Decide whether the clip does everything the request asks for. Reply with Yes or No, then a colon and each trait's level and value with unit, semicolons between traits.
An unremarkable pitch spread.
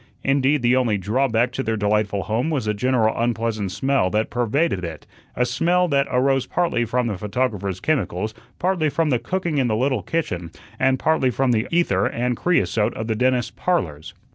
Yes: average, 4.3 semitones